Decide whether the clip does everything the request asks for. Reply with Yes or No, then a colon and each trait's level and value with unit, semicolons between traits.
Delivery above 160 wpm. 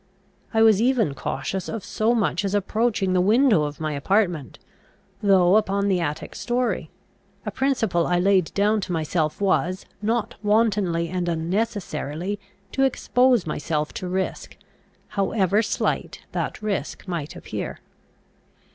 No: slow, 135 wpm